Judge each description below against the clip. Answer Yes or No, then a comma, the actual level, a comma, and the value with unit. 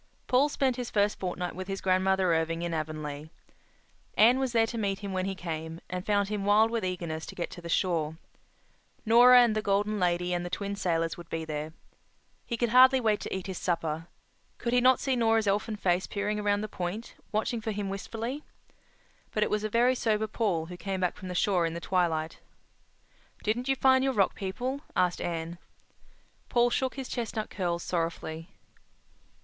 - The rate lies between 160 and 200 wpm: Yes, average, 195 wpm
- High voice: Yes, high, 195 Hz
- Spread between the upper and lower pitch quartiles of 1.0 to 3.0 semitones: No, average, 4.5 semitones